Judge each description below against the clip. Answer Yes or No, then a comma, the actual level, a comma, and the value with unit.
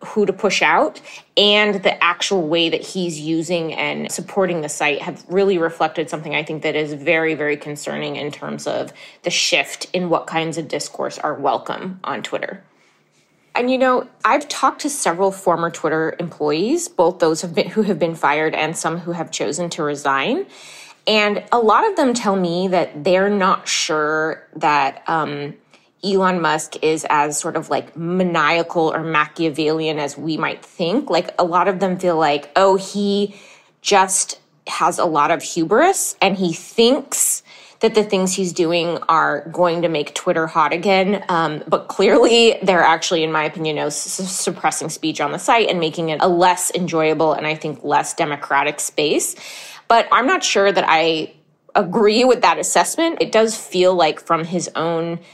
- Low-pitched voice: No, medium, 170 Hz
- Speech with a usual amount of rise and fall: Yes, average, 3.7 semitones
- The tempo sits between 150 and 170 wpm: No, average, 180 wpm